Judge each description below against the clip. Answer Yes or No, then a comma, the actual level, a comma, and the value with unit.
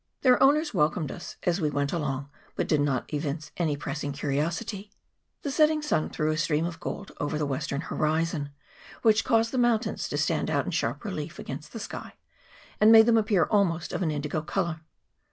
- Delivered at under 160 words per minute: No, average, 190 wpm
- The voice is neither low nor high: Yes, medium, 160 Hz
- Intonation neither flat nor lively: No, wide, 6.6 semitones